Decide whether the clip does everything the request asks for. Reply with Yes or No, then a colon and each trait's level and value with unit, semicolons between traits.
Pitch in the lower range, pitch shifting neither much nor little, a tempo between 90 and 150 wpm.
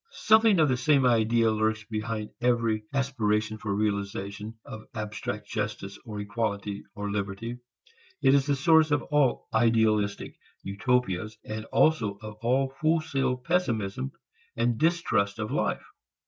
Yes: low, 110 Hz; average, 4.0 semitones; slow, 135 wpm